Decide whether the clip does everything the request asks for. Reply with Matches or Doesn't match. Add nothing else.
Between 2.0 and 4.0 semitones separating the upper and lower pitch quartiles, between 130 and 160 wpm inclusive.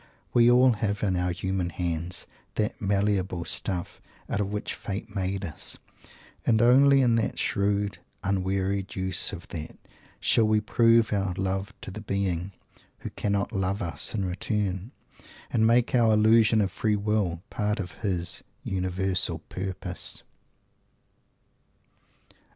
Matches